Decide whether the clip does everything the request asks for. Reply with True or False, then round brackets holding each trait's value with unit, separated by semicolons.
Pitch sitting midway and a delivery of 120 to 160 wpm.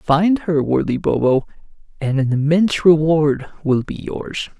True (155 Hz; 145 wpm)